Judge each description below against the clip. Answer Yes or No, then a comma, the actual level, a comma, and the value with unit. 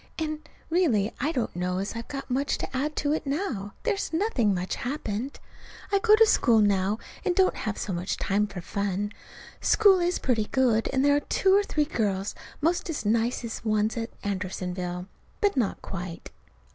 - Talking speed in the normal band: Yes, average, 190 wpm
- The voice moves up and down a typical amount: No, wide, 7.3 semitones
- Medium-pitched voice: No, high, 230 Hz